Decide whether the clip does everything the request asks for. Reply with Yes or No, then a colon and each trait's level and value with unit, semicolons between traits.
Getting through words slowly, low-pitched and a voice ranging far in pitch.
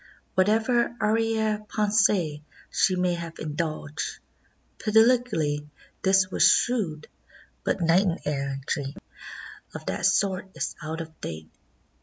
No: slow, 105 wpm; medium, 185 Hz; wide, 5.7 semitones